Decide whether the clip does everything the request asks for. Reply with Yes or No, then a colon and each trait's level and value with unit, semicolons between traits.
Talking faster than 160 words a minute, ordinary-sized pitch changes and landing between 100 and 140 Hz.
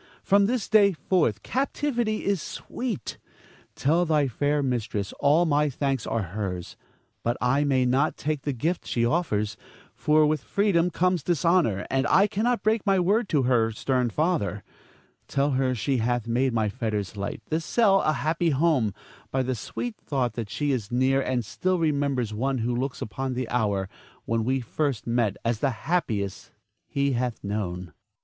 No: average, 170 wpm; wide, 6.2 semitones; low, 135 Hz